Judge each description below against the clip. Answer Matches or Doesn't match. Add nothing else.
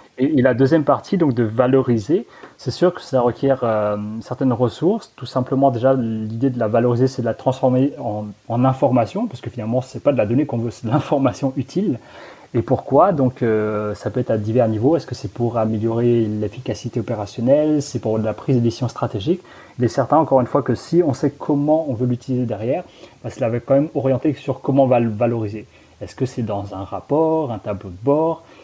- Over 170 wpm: Matches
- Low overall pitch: Matches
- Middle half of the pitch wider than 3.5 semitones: Doesn't match